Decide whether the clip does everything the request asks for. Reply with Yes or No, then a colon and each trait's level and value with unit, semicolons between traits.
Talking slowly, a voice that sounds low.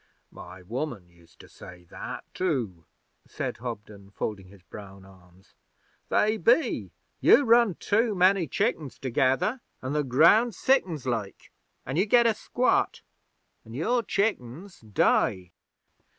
Yes: slow, 130 wpm; low, 130 Hz